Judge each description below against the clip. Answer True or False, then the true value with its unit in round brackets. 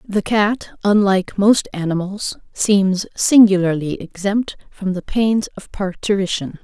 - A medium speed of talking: False (120 wpm)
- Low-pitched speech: False (200 Hz)